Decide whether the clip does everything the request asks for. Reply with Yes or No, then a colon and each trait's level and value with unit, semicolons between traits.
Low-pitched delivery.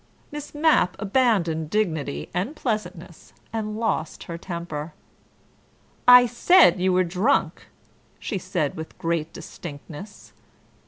No: medium, 185 Hz